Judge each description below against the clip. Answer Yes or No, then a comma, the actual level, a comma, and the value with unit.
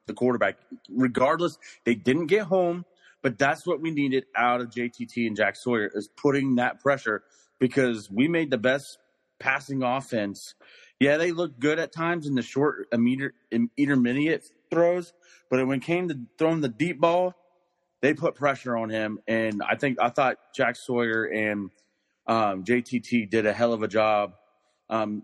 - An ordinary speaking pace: Yes, average, 170 wpm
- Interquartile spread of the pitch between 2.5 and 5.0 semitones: No, wide, 5.5 semitones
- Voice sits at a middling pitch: No, low, 130 Hz